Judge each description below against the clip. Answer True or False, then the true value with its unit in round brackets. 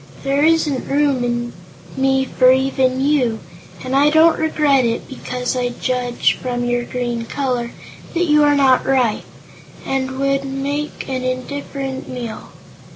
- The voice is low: False (265 Hz)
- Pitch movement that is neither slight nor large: False (2.2 semitones)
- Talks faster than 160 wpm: False (145 wpm)